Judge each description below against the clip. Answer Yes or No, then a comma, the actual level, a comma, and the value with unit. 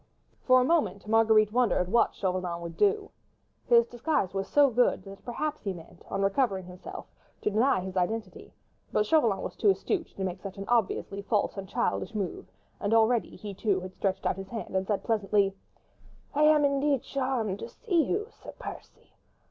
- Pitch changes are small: No, average, 4.9 semitones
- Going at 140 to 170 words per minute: No, average, 185 wpm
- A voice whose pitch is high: Yes, high, 215 Hz